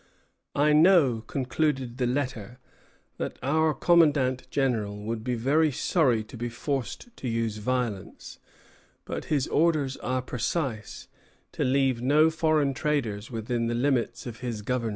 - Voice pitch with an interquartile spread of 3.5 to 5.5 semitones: Yes, average, 4.0 semitones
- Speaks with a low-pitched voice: Yes, low, 130 Hz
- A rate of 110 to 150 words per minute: Yes, average, 140 wpm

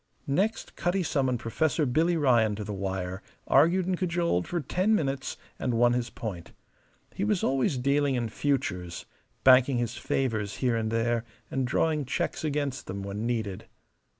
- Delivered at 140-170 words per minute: Yes, average, 160 wpm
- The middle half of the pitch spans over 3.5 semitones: Yes, wide, 5.4 semitones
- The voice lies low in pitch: Yes, low, 130 Hz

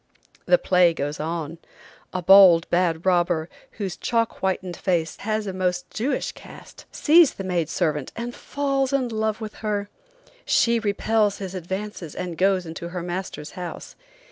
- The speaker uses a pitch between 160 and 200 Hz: Yes, medium, 185 Hz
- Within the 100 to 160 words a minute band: Yes, average, 155 wpm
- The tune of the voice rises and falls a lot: No, average, 4.0 semitones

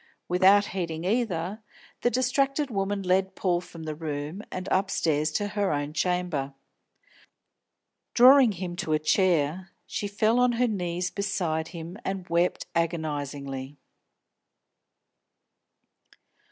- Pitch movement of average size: Yes, average, 4.2 semitones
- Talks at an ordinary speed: No, slow, 115 wpm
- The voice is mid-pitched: Yes, medium, 180 Hz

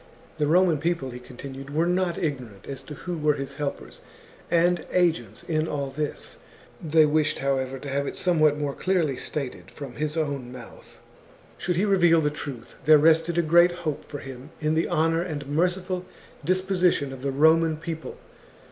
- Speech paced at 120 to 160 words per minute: No, average, 175 wpm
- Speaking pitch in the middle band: Yes, medium, 155 Hz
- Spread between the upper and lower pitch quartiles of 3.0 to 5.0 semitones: Yes, average, 3.5 semitones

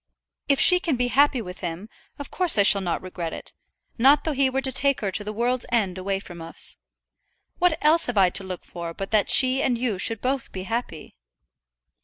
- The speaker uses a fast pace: Yes, fast, 220 wpm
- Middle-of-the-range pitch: No, high, 230 Hz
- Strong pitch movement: Yes, wide, 6.1 semitones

